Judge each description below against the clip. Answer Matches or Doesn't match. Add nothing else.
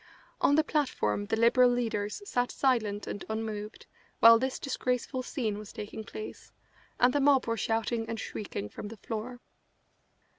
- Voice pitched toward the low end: Doesn't match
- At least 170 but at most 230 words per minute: Doesn't match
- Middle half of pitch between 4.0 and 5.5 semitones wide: Doesn't match